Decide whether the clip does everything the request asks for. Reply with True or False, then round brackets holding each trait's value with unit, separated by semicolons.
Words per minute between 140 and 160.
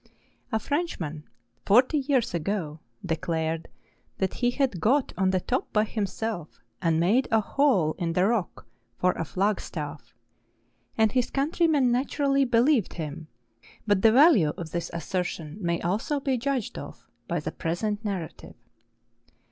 True (150 wpm)